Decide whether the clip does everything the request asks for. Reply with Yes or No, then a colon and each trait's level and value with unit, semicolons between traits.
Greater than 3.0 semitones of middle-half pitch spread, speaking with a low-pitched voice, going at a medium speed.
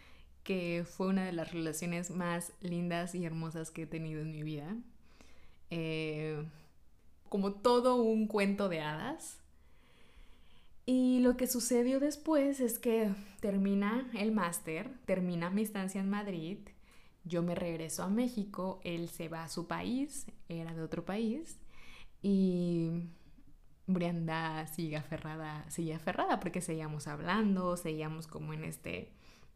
No: average, 4.3 semitones; medium, 175 Hz; average, 135 wpm